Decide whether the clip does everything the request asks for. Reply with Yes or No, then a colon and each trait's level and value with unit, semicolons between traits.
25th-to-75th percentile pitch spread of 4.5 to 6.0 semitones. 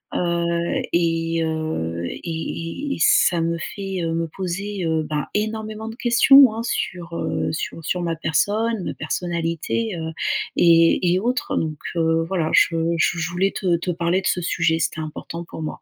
No: average, 2.8 semitones